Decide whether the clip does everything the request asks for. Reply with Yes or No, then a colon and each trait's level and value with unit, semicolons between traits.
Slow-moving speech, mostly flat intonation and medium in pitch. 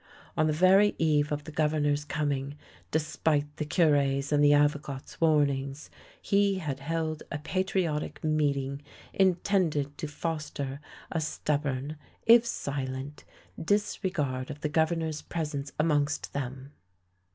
Yes: slow, 125 wpm; narrow, 2.2 semitones; medium, 150 Hz